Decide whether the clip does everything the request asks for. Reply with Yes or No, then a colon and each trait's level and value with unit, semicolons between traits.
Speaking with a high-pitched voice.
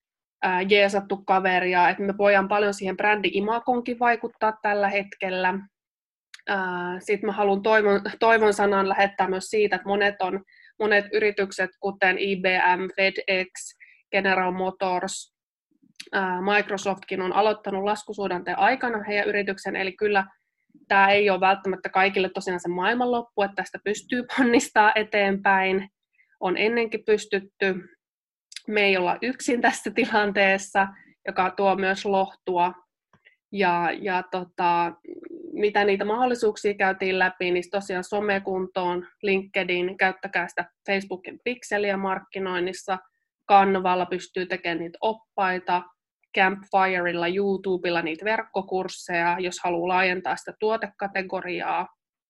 Yes: high, 195 Hz